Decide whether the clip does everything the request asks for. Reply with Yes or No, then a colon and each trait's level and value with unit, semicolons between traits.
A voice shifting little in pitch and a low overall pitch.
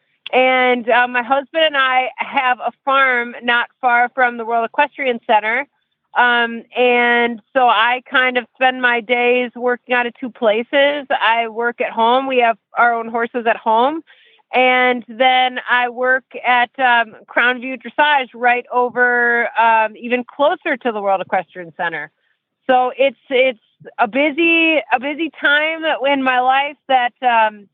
No: narrow, 2.0 semitones; high, 245 Hz